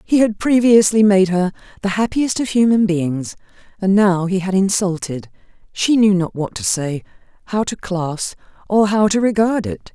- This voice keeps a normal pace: Yes, average, 170 wpm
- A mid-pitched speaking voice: No, high, 195 Hz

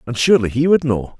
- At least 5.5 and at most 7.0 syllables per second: Yes, 6.9 syllables/s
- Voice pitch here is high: No, low, 130 Hz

